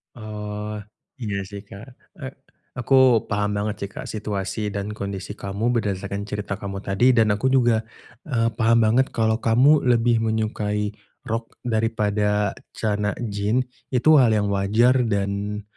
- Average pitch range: No, narrow, 2.0 semitones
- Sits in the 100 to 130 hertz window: Yes, low, 105 Hz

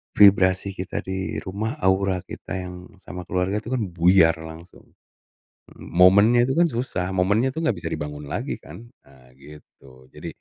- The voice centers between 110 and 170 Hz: No, very low, 95 Hz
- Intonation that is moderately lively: Yes, average, 3.5 semitones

